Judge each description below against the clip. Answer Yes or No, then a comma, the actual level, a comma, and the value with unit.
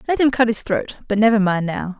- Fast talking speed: Yes, fast, 240 wpm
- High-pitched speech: Yes, high, 220 Hz